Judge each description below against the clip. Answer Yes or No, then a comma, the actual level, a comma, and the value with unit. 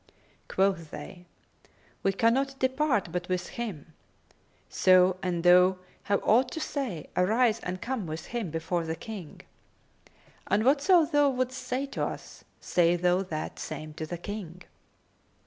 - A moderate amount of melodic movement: No, wide, 6.2 semitones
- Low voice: No, medium, 185 Hz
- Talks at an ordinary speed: Yes, average, 145 wpm